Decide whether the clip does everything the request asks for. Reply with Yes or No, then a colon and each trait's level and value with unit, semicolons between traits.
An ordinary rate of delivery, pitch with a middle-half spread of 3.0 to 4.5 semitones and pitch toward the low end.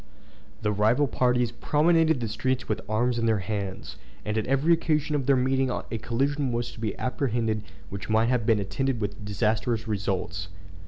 Yes: average, 175 wpm; average, 3.7 semitones; low, 115 Hz